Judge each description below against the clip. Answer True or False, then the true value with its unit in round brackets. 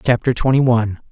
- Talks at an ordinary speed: True (160 wpm)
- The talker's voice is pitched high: False (120 Hz)